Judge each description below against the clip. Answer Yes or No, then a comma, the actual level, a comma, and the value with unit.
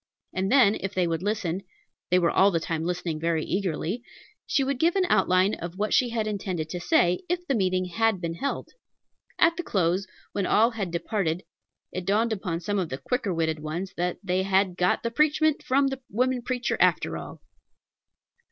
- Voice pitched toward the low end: No, high, 190 Hz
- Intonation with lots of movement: No, average, 4.9 semitones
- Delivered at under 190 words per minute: No, average, 195 wpm